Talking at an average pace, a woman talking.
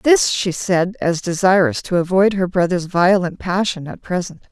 Yes: average, 175 wpm; female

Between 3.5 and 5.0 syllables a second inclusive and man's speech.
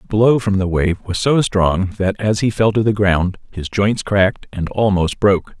Yes: 4.6 syllables/s; male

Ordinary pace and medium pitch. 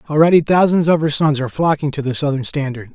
No: fast, 225 wpm; medium, 145 Hz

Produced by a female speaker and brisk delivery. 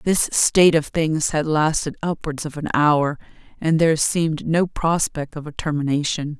No: female; average, 170 wpm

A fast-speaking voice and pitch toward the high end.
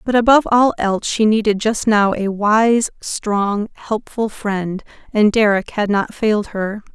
No: average, 165 wpm; high, 215 Hz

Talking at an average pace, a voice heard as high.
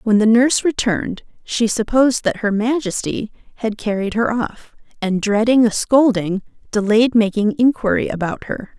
Yes: average, 150 wpm; high, 220 Hz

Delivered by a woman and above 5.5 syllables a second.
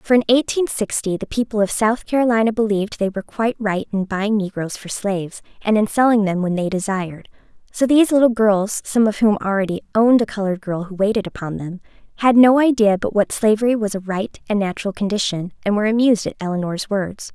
Yes: female; 6.1 syllables/s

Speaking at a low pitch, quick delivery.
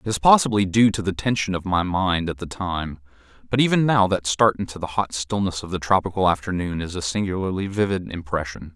Yes: very low, 95 Hz; fast, 210 wpm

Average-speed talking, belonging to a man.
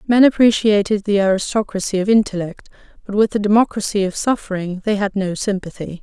No: average, 160 wpm; female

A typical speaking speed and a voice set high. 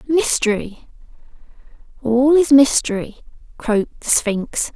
No: slow, 90 wpm; very high, 250 Hz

